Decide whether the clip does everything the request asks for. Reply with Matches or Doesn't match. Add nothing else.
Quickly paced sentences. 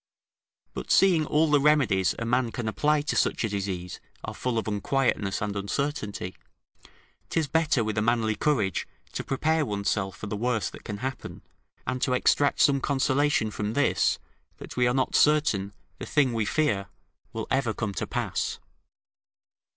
Doesn't match